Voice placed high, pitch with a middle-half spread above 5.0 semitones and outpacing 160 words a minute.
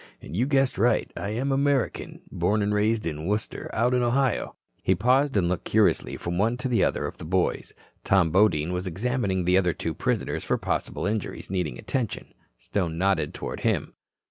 No: low, 100 Hz; wide, 5.4 semitones; average, 195 wpm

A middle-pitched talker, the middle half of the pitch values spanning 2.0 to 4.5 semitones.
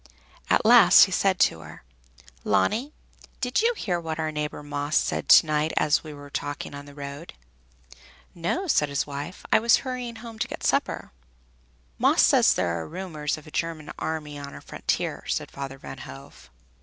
No: medium, 155 Hz; average, 5.0 semitones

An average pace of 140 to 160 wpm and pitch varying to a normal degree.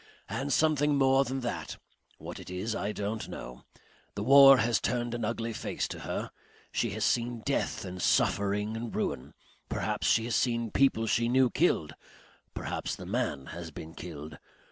No: average, 170 wpm; average, 4.1 semitones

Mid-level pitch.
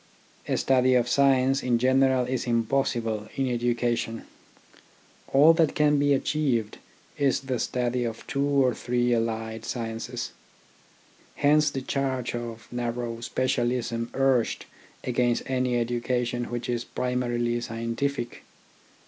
No: low, 125 Hz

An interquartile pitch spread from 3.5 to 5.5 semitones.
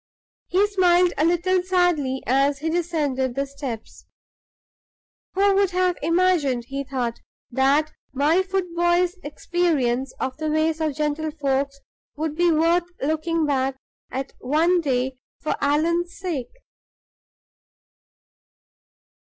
Yes: average, 4.2 semitones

